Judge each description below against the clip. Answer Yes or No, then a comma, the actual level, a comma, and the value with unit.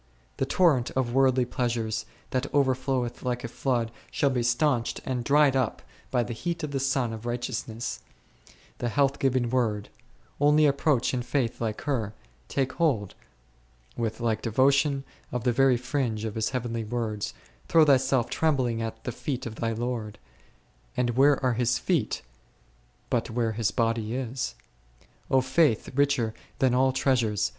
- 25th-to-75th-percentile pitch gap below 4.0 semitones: Yes, average, 2.7 semitones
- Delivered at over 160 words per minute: No, average, 155 wpm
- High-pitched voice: No, low, 125 Hz